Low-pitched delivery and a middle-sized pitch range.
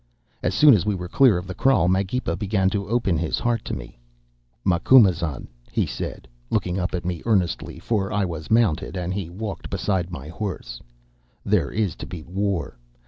Yes: very low, 95 Hz; average, 3.4 semitones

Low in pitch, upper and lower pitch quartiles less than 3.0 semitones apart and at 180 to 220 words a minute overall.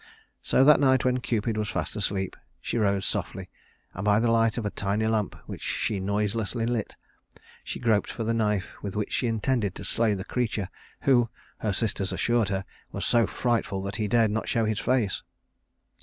Yes: low, 110 Hz; narrow, 2.5 semitones; average, 190 wpm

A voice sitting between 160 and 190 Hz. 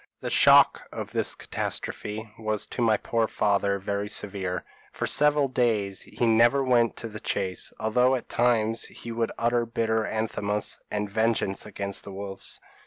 No: low, 110 Hz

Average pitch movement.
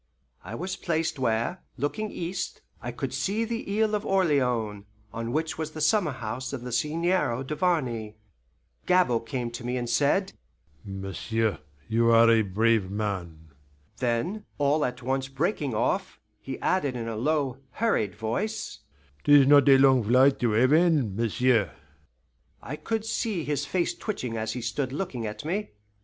No: wide, 6.2 semitones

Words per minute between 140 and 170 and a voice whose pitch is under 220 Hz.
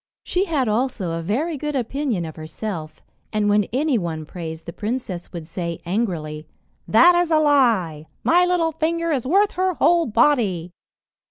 No: average, 165 wpm; high, 230 Hz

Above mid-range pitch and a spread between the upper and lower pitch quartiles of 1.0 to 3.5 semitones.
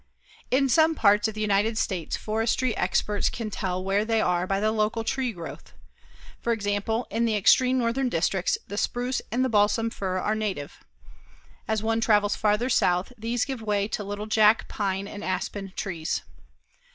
Yes: high, 215 Hz; narrow, 2.4 semitones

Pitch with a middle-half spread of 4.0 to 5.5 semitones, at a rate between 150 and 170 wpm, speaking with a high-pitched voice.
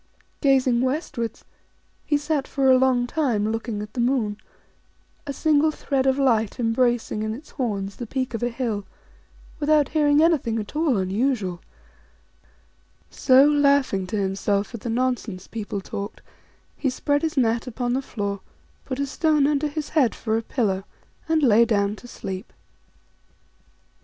Yes: average, 4.6 semitones; average, 155 wpm; high, 245 Hz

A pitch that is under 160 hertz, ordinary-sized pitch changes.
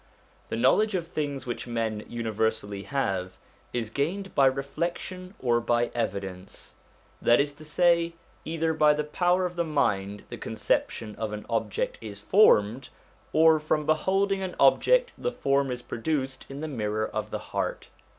No: low, 135 Hz; wide, 6.8 semitones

